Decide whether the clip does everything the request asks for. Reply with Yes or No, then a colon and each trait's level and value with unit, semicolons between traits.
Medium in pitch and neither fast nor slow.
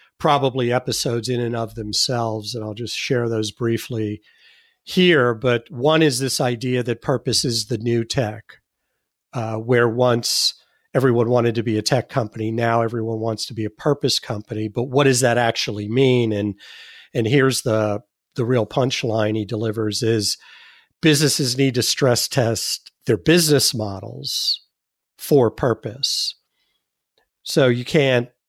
No: low, 120 Hz; average, 150 wpm